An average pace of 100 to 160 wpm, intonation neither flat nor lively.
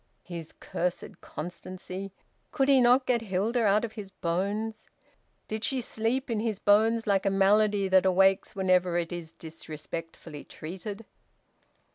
Yes: average, 140 wpm; average, 3.7 semitones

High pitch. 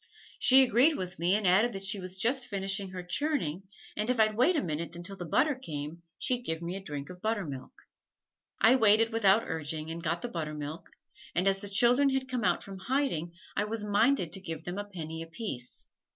Yes: high, 195 Hz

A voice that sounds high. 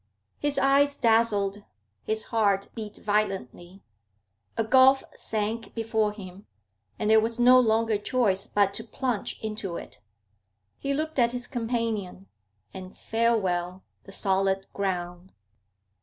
Yes: high, 215 Hz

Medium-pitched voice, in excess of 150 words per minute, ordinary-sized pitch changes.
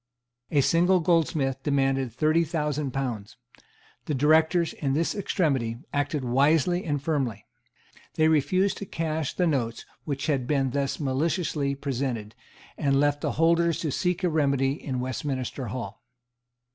No: medium, 145 Hz; average, 140 wpm; average, 3.2 semitones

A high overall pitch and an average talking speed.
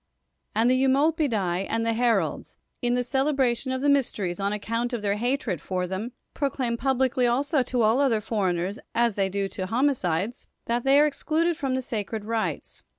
Yes: high, 235 Hz; average, 190 wpm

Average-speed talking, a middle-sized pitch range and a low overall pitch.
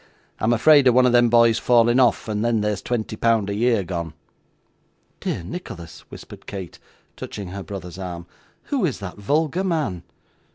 Yes: average, 170 wpm; average, 4.3 semitones; low, 115 Hz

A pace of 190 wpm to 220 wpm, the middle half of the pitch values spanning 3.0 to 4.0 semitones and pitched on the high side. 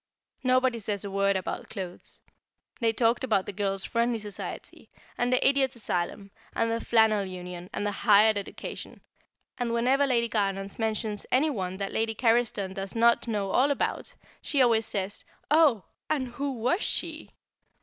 No: average, 160 wpm; average, 3.7 semitones; high, 225 Hz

